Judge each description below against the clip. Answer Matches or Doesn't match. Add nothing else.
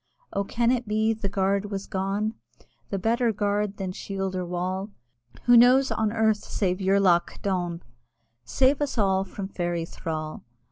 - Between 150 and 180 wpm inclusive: Matches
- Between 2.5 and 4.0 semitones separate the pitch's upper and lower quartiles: Matches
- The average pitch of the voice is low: Doesn't match